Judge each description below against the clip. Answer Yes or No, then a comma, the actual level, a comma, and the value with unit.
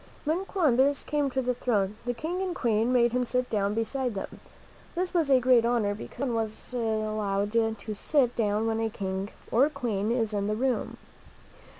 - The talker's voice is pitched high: Yes, high, 235 Hz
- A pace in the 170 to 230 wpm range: Yes, average, 195 wpm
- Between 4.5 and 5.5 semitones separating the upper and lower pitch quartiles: No, average, 3.6 semitones